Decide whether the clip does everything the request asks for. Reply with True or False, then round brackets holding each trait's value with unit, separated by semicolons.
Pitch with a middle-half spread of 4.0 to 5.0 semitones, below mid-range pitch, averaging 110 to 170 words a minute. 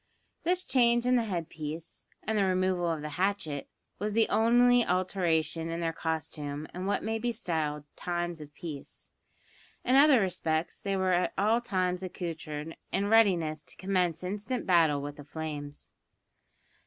False (4.6 semitones; 180 Hz; 165 wpm)